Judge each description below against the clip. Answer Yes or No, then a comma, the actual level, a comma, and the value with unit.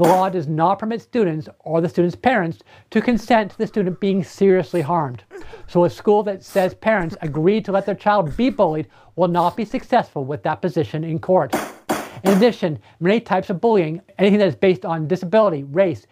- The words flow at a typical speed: Yes, average, 195 wpm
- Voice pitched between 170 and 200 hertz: Yes, medium, 185 Hz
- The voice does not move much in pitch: No, average, 4.1 semitones